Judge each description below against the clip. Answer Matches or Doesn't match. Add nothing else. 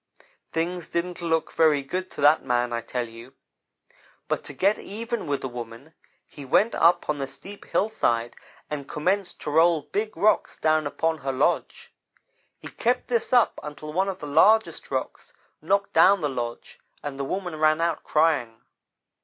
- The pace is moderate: Matches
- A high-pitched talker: Doesn't match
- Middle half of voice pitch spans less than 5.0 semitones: Doesn't match